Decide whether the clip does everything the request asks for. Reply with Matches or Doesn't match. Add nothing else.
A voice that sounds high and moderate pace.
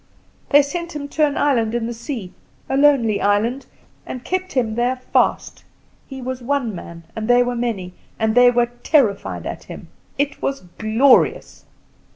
Matches